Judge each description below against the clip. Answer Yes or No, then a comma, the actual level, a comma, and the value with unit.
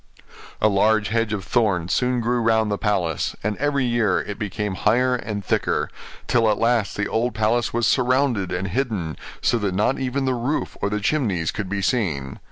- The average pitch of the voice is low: Yes, low, 110 Hz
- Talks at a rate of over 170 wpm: Yes, average, 190 wpm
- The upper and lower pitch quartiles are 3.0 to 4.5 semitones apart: Yes, average, 3.5 semitones